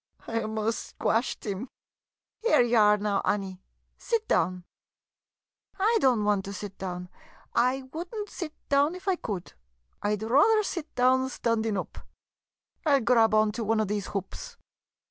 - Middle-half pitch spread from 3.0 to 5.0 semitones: No, wide, 5.5 semitones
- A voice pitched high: Yes, high, 225 Hz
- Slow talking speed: No, average, 175 wpm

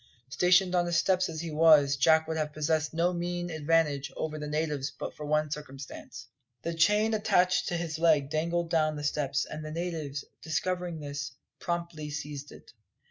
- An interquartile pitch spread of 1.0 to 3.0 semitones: Yes, narrow, 2.5 semitones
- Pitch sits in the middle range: Yes, medium, 160 Hz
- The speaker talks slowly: No, average, 180 wpm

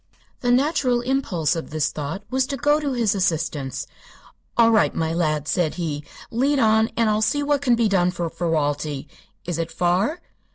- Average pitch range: No, wide, 7.3 semitones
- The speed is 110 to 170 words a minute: No, average, 180 wpm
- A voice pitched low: No, high, 195 Hz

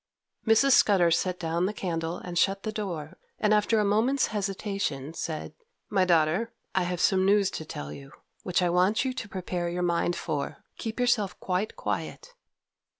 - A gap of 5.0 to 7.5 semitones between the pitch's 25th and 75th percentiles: No, average, 3.7 semitones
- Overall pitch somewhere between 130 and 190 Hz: Yes, medium, 185 Hz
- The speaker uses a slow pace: No, average, 175 wpm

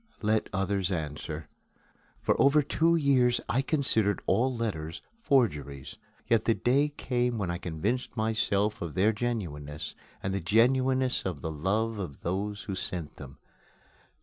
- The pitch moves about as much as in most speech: No, wide, 6.1 semitones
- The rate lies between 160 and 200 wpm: No, average, 145 wpm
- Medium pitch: No, low, 105 Hz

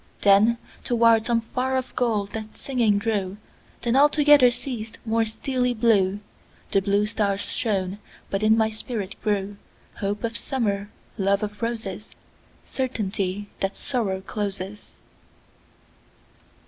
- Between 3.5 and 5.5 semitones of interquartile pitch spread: No, average, 2.8 semitones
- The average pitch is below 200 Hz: No, high, 215 Hz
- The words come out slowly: Yes, slow, 110 wpm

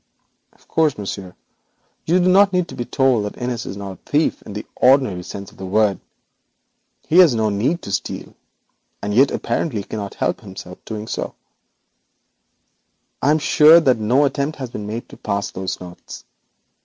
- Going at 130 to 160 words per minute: No, average, 175 wpm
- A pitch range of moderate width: No, wide, 6.4 semitones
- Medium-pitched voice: No, low, 115 Hz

